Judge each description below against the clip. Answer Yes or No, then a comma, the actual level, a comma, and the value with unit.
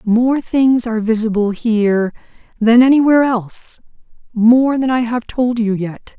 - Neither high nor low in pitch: No, high, 230 Hz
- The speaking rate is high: No, slow, 135 wpm